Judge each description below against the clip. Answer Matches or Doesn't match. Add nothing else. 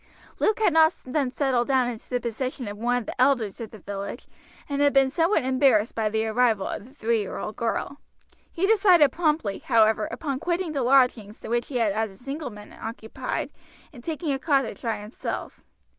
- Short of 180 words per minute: Doesn't match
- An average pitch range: Matches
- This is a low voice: Doesn't match